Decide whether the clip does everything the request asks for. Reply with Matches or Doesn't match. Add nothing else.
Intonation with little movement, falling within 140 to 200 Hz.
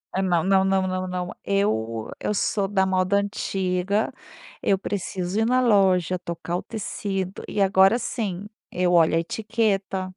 Matches